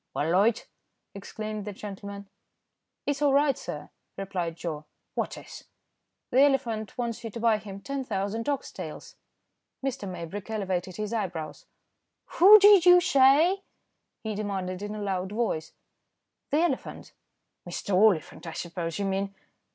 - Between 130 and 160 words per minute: Yes, average, 140 wpm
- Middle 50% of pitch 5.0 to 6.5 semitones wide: Yes, wide, 5.5 semitones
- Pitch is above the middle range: Yes, high, 210 Hz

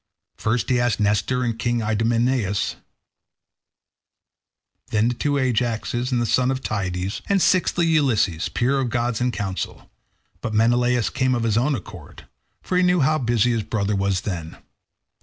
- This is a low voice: Yes, low, 120 Hz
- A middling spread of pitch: Yes, average, 3.2 semitones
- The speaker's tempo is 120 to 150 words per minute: No, average, 160 wpm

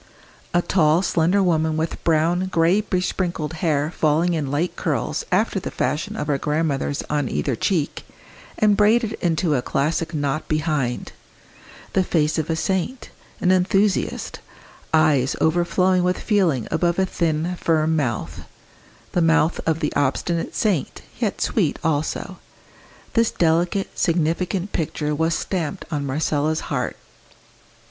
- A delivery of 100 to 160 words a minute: Yes, slow, 135 wpm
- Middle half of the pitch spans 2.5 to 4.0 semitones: Yes, average, 2.9 semitones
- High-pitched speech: No, medium, 165 Hz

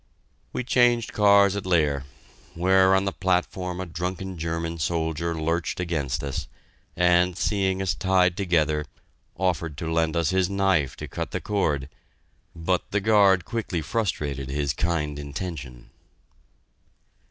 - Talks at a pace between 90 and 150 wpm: Yes, slow, 135 wpm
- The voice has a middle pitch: No, very low, 90 Hz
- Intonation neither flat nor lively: Yes, average, 3.3 semitones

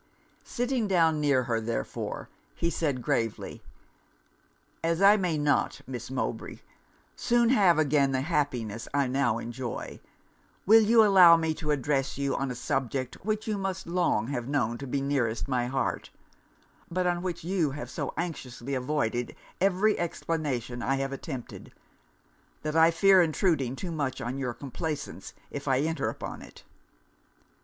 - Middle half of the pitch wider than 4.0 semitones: Yes, average, 5.1 semitones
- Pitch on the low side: No, medium, 145 Hz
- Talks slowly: No, average, 150 wpm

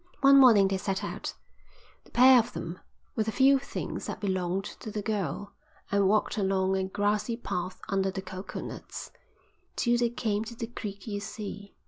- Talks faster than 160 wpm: Yes, average, 175 wpm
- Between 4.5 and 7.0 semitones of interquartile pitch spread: No, average, 3.2 semitones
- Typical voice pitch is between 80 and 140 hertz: No, high, 205 Hz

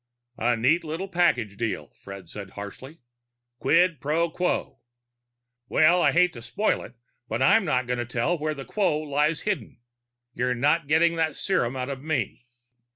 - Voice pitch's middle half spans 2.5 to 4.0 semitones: No, wide, 5.6 semitones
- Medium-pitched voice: Yes, medium, 150 Hz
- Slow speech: No, average, 165 wpm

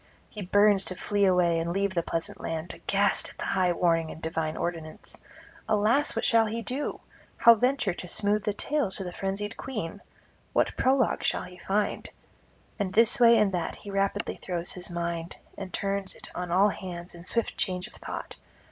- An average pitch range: Yes, average, 3.4 semitones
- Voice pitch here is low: No, high, 195 Hz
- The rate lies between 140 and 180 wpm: No, average, 190 wpm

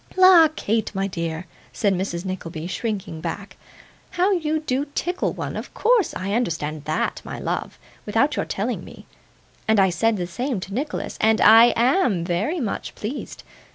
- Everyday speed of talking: Yes, average, 165 wpm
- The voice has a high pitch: Yes, high, 210 Hz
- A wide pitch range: Yes, wide, 7.5 semitones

